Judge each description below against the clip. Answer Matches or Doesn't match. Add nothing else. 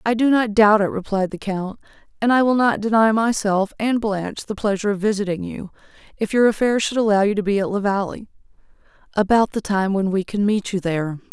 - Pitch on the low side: Doesn't match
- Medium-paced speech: Doesn't match